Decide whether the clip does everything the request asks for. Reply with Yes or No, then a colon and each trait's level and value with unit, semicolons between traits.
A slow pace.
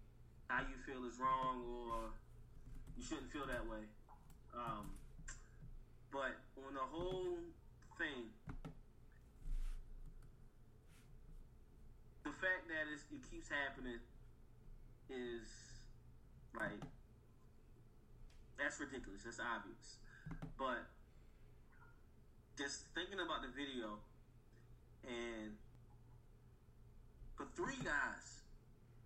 Yes: slow, 85 wpm